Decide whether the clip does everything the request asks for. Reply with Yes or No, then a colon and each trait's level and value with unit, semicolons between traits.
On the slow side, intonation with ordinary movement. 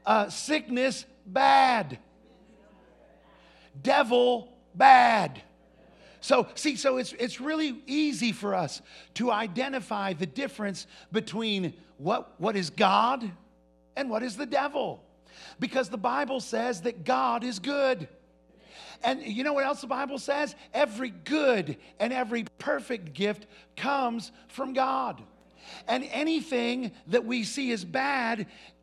Yes: slow, 125 wpm; average, 4.6 semitones